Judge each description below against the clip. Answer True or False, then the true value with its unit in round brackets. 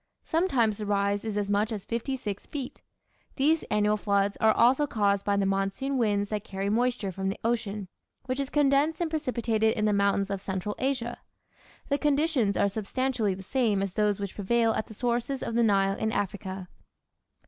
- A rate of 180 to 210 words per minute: True (190 wpm)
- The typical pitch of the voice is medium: False (215 Hz)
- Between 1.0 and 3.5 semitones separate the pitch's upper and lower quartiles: False (4.0 semitones)